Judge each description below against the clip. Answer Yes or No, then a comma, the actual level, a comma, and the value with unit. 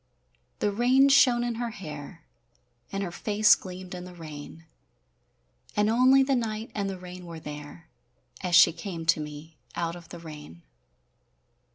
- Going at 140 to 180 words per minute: Yes, average, 160 wpm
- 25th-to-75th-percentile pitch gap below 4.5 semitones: No, average, 4.9 semitones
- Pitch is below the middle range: No, medium, 180 Hz